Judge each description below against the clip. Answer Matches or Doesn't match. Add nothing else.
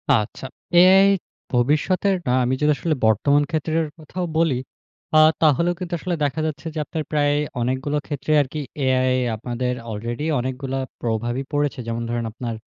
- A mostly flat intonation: Doesn't match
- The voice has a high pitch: Doesn't match